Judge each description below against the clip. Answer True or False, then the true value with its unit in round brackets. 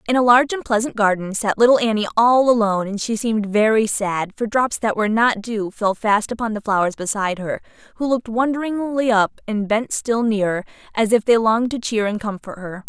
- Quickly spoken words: True (215 wpm)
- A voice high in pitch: True (220 Hz)